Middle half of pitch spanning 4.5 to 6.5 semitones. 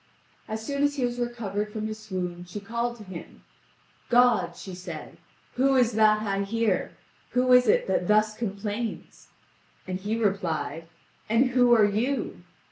No: average, 3.4 semitones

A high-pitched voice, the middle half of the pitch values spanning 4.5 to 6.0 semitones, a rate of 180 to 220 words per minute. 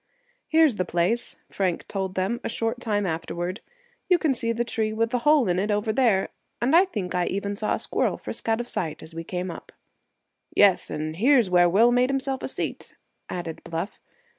Yes: high, 210 Hz; average, 5.0 semitones; fast, 205 wpm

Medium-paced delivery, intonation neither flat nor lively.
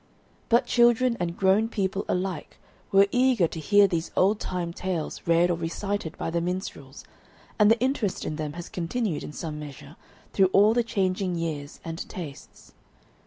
Yes: average, 165 wpm; average, 3.9 semitones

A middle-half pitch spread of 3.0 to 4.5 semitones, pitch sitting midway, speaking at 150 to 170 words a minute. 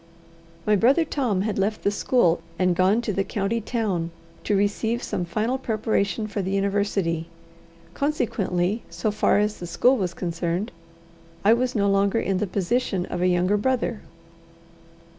No: average, 3.4 semitones; high, 205 Hz; average, 160 wpm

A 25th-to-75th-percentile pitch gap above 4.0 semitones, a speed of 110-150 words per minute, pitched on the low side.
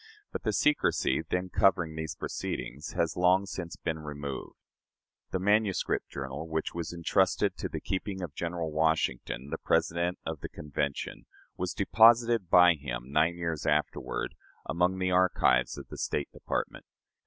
No: average, 3.5 semitones; average, 145 wpm; very low, 85 Hz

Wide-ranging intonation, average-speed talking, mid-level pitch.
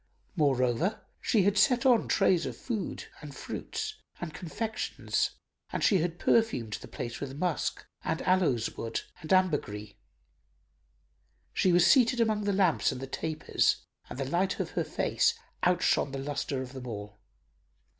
Yes: wide, 7.3 semitones; average, 155 wpm; medium, 170 Hz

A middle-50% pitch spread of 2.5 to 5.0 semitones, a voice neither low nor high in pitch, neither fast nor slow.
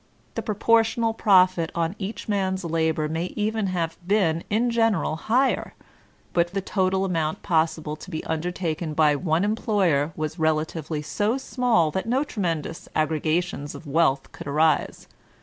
Yes: average, 4.6 semitones; medium, 175 Hz; average, 145 wpm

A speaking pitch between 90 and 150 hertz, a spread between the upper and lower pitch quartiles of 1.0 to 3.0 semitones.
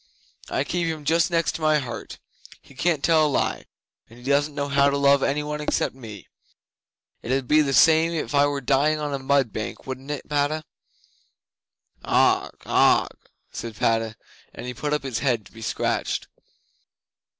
Yes: medium, 140 Hz; narrow, 2.6 semitones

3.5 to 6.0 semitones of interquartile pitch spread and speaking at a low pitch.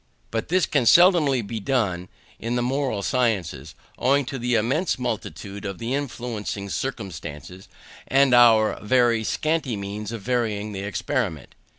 Yes: average, 4.4 semitones; low, 115 Hz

